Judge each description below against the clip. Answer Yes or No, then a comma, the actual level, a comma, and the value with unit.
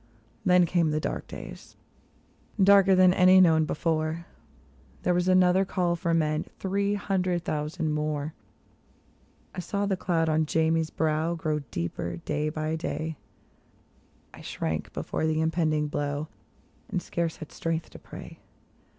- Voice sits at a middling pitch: Yes, medium, 160 Hz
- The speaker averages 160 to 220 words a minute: No, average, 140 wpm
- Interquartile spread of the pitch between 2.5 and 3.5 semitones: Yes, average, 2.8 semitones